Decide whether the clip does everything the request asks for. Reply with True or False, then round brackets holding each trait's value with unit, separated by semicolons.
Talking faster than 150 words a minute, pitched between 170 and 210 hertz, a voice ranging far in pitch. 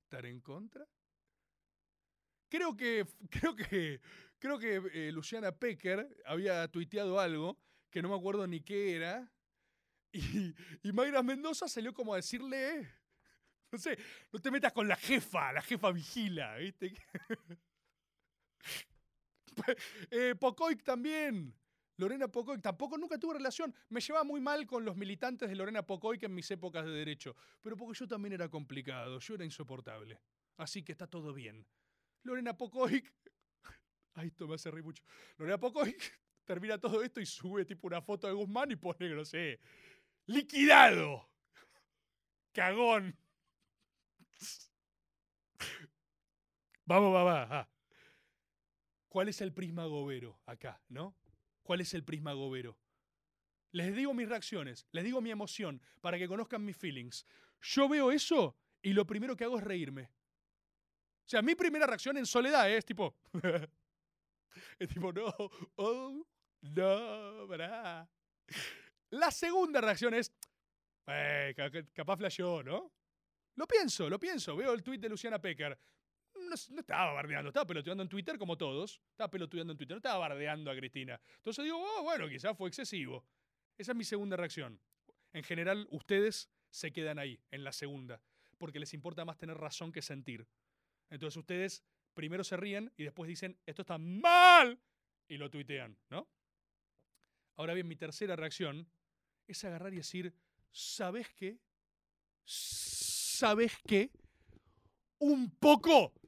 False (145 wpm; 190 Hz; 7.1 semitones)